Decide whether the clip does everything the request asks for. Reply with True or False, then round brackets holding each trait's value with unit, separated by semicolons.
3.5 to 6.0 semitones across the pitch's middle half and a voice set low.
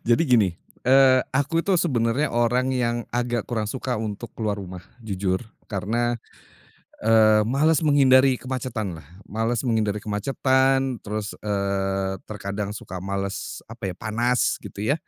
True (4.0 semitones; 115 Hz)